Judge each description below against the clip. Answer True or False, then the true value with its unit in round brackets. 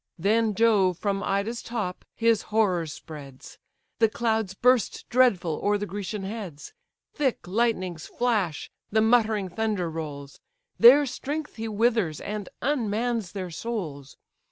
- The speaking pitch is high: True (210 Hz)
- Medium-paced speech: False (130 wpm)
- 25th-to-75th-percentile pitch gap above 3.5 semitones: True (4.1 semitones)